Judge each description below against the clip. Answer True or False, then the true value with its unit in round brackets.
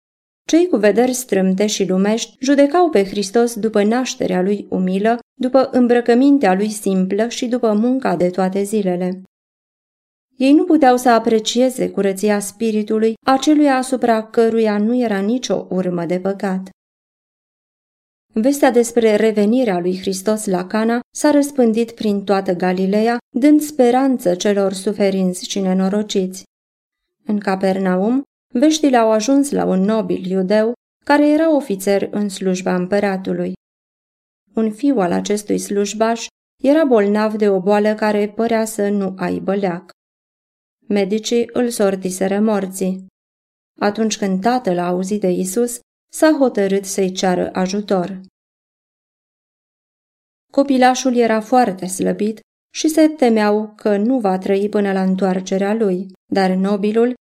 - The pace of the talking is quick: False (125 wpm)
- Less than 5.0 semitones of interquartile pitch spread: True (4.0 semitones)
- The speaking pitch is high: True (215 Hz)